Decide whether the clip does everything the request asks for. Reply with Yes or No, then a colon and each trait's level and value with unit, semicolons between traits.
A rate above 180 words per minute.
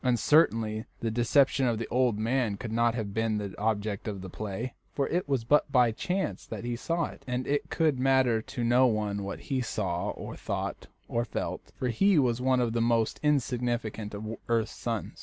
Yes: fast, 205 wpm